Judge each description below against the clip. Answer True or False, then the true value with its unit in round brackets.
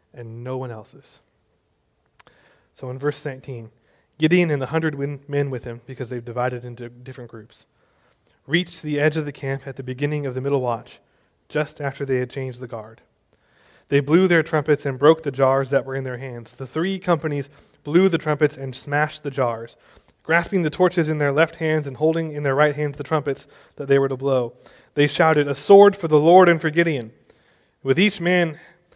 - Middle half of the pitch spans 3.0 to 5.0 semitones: True (3.4 semitones)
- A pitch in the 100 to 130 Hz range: False (140 Hz)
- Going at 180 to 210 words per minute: True (200 wpm)